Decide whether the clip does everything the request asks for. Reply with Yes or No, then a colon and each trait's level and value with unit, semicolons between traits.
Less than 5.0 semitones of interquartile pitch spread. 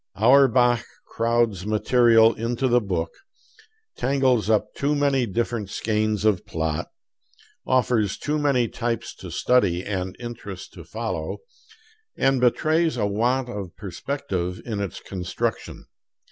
Yes: average, 3.8 semitones